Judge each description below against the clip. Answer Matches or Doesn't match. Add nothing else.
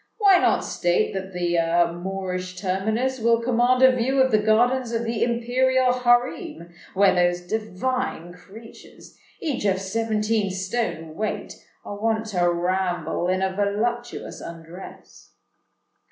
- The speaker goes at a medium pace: Doesn't match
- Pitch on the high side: Matches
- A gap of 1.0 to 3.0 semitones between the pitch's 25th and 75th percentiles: Doesn't match